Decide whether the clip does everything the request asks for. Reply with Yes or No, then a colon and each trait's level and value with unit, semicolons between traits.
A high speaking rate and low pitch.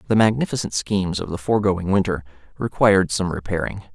No: average, 150 wpm; very low, 95 Hz